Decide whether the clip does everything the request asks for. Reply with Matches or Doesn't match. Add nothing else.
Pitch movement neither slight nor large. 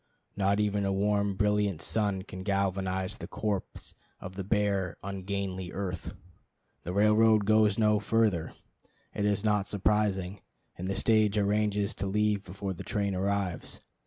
Doesn't match